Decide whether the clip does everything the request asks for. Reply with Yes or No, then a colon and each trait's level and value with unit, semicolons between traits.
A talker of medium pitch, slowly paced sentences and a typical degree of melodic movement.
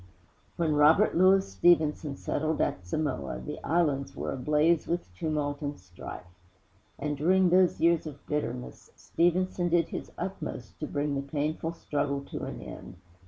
No: medium, 150 Hz; average, 155 wpm; average, 3.5 semitones